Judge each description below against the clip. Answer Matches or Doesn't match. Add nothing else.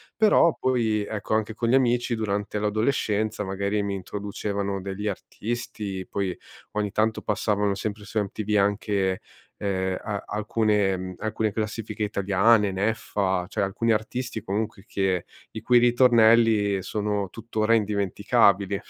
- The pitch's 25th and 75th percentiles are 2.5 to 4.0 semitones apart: Doesn't match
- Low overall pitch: Matches